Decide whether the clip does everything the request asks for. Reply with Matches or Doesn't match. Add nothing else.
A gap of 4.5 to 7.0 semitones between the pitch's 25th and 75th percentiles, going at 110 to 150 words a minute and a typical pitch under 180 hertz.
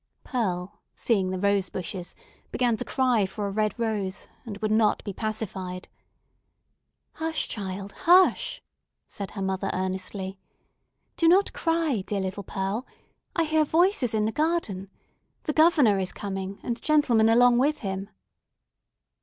Doesn't match